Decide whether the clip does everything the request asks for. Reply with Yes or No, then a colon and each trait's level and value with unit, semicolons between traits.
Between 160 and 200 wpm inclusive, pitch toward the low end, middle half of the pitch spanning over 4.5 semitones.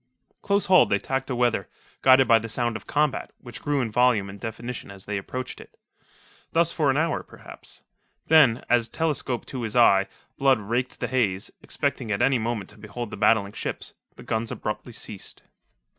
No: average, 185 wpm; low, 120 Hz; average, 3.7 semitones